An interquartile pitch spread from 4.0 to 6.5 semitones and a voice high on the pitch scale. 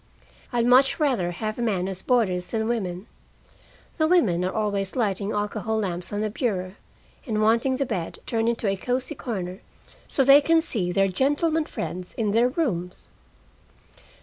Yes: average, 5.0 semitones; high, 215 Hz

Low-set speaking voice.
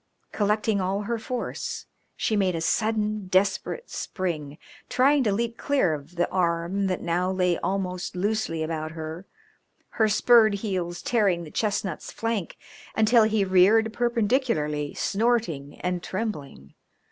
No: high, 195 Hz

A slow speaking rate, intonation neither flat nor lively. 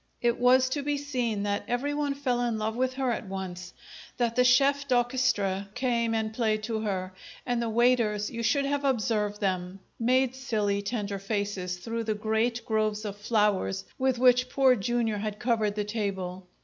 No: average, 175 wpm; average, 3.4 semitones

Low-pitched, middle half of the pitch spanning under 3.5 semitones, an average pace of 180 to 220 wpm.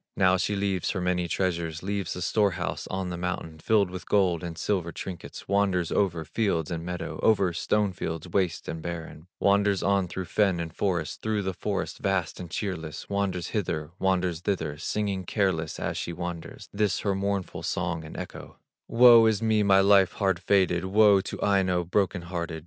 Yes: very low, 95 Hz; average, 2.7 semitones; average, 185 wpm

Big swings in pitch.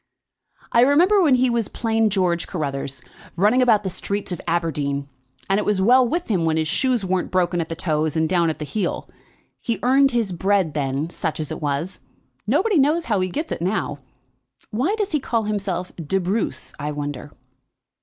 Yes: wide, 6.9 semitones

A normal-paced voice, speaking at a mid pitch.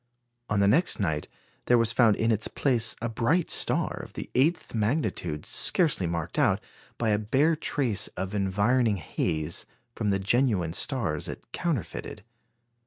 No: average, 155 wpm; low, 110 Hz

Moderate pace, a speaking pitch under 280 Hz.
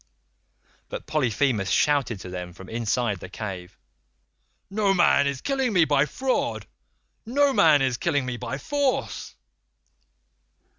No: slow, 120 wpm; medium, 140 Hz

